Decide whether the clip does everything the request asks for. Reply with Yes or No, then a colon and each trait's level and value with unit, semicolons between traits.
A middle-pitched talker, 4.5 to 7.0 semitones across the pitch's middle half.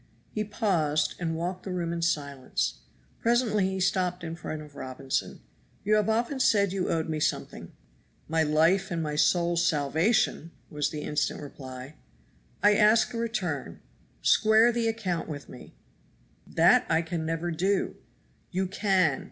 Yes: medium, 170 Hz; average, 4.8 semitones